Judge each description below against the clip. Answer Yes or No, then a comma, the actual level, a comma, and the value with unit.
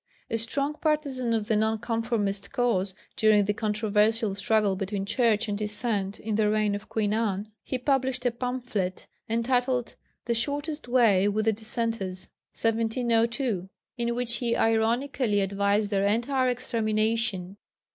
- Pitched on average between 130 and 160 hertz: No, high, 225 Hz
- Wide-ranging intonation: No, average, 2.9 semitones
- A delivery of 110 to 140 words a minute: Yes, slow, 135 wpm